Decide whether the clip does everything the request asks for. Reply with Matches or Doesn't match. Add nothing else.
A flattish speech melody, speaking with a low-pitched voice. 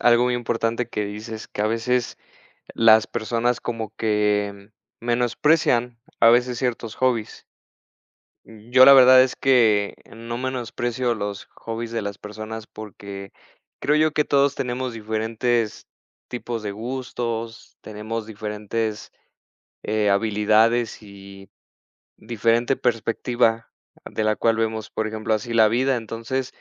Matches